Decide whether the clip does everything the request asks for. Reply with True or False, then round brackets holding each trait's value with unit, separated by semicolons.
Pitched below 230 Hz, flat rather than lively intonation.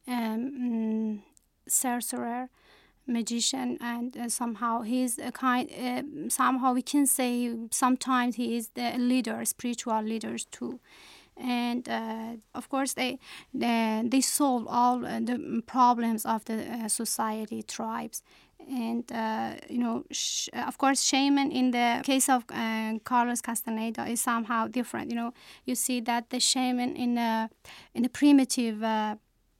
False (245 Hz; 1.9 semitones)